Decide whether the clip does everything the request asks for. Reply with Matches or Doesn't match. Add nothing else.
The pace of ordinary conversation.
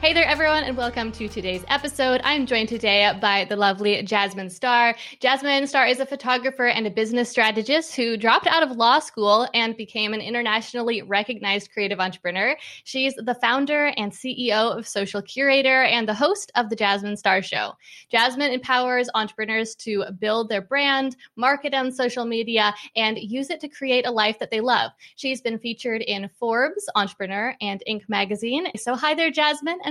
Matches